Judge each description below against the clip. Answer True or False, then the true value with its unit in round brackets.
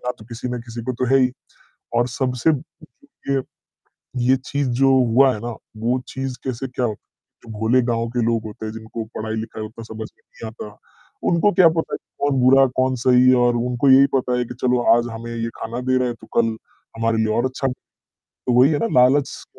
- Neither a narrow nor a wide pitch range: False (2.3 semitones)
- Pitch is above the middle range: False (125 Hz)